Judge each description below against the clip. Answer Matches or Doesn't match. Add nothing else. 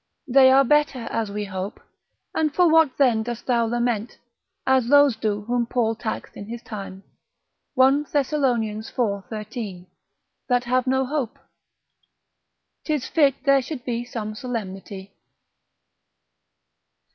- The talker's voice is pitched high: Matches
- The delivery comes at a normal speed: Doesn't match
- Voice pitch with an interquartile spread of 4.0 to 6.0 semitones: Doesn't match